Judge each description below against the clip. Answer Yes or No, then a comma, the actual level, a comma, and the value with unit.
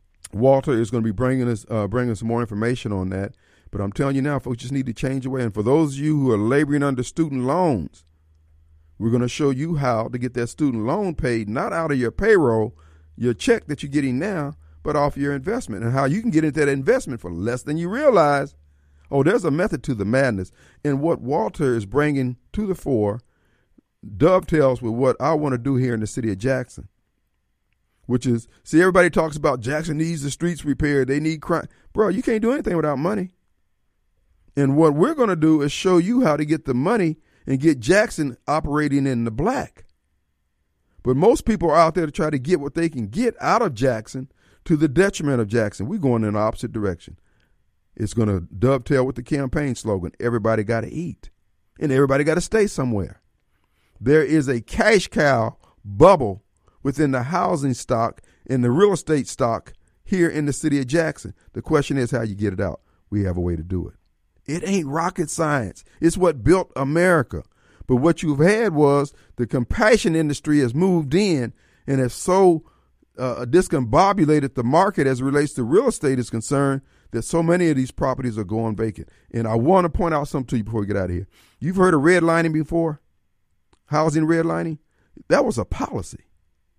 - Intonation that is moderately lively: No, wide, 6.0 semitones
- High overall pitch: No, low, 135 Hz